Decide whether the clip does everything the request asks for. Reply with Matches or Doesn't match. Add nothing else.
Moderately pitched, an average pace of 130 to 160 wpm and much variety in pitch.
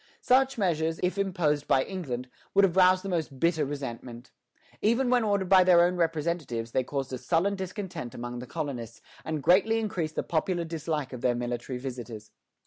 Doesn't match